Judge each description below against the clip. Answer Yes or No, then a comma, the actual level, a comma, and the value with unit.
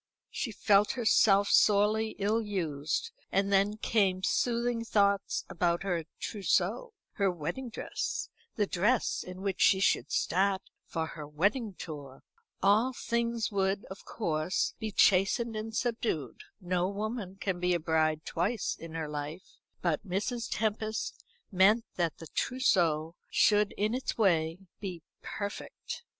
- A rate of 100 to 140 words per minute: Yes, slow, 135 wpm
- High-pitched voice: Yes, high, 195 Hz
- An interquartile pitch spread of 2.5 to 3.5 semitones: No, average, 4.0 semitones